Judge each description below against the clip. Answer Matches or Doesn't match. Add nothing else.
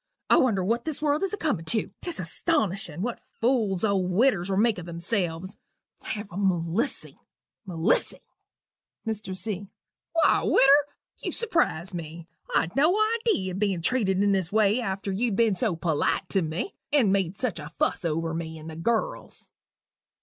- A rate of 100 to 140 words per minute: Doesn't match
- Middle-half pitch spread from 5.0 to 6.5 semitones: Matches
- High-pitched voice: Matches